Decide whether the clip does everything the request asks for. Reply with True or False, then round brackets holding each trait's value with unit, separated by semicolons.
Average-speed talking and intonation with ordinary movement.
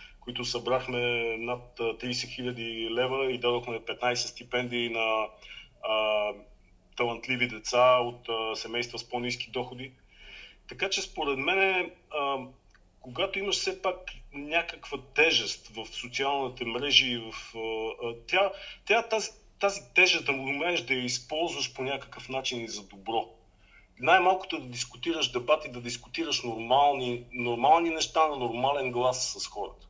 True (130 wpm; 3.3 semitones)